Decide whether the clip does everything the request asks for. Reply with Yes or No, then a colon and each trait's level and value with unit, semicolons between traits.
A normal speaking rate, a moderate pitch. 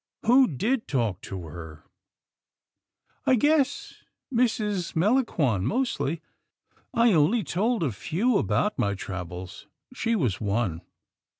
No: slow, 120 wpm; medium, 170 Hz